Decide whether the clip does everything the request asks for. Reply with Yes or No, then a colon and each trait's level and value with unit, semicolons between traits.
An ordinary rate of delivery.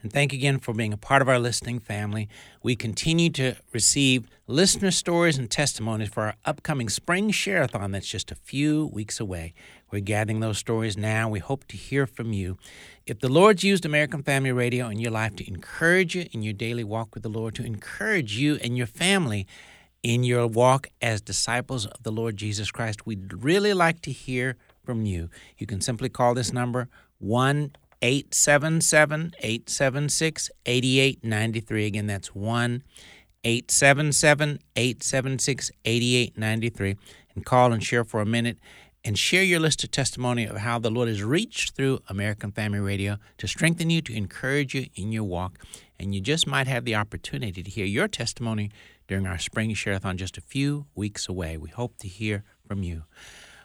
Yes: average, 175 wpm